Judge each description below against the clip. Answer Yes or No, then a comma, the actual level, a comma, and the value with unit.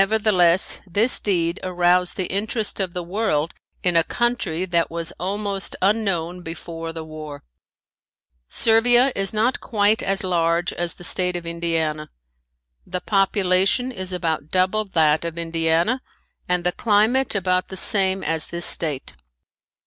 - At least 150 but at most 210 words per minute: No, average, 140 wpm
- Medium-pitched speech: Yes, medium, 180 Hz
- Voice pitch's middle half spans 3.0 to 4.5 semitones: Yes, average, 3.3 semitones